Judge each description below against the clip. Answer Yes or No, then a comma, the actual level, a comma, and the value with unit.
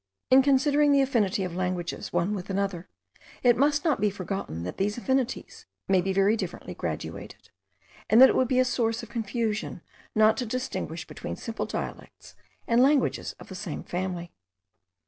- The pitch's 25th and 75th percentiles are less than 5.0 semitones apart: No, wide, 5.6 semitones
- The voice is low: No, high, 220 Hz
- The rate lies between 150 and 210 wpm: Yes, average, 170 wpm